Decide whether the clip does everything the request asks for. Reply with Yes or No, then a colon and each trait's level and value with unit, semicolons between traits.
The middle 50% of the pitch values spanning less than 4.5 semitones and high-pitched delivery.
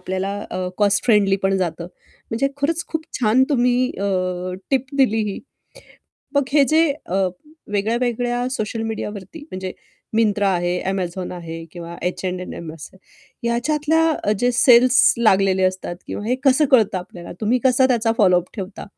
No: average, 5.1 semitones; high, 215 Hz